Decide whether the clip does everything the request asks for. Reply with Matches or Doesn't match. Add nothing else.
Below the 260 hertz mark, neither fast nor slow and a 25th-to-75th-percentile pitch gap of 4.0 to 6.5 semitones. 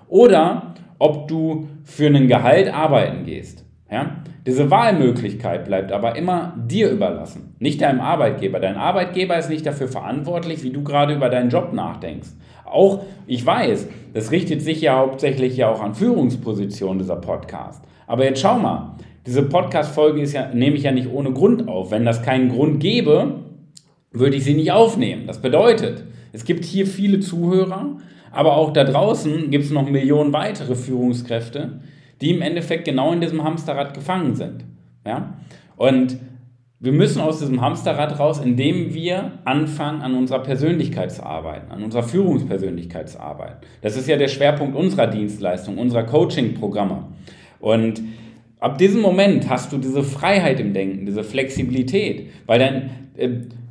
Matches